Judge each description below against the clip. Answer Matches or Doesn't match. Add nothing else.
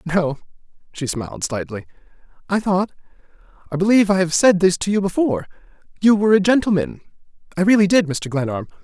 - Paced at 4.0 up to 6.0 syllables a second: Doesn't match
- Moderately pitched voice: Matches